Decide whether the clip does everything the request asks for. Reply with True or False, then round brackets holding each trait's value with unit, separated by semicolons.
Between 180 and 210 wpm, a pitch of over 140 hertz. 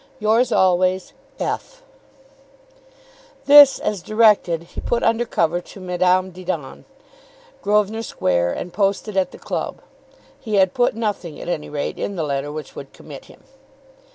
False (145 wpm; 185 Hz)